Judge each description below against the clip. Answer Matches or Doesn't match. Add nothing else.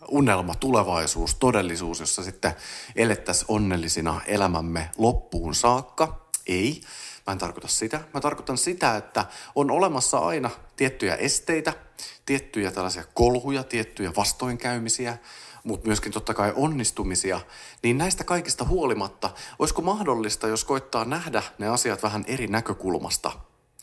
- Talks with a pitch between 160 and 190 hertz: Doesn't match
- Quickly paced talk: Doesn't match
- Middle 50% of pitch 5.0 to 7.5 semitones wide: Matches